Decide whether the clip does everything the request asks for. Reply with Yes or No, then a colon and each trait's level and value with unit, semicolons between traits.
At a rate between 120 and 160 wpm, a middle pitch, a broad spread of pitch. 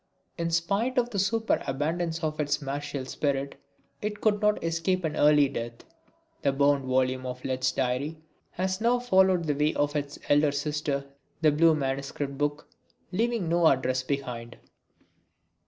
No: average, 150 wpm; medium, 150 Hz; average, 4.2 semitones